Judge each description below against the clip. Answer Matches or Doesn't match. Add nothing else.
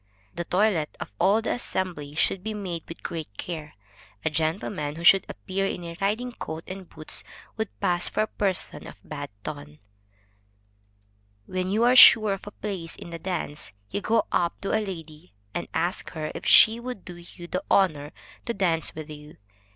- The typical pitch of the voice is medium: Matches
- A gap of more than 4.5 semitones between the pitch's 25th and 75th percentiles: Doesn't match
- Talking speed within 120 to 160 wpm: Doesn't match